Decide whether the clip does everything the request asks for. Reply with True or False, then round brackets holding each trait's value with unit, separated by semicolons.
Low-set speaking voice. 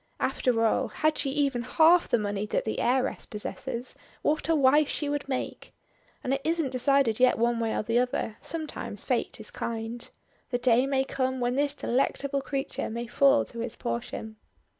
False (255 Hz)